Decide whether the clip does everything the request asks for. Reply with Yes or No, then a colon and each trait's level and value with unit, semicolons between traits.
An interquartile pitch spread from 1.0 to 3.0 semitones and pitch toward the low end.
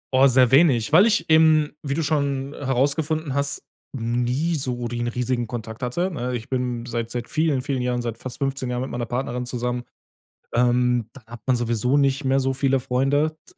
Yes: average, 2.7 semitones; low, 130 Hz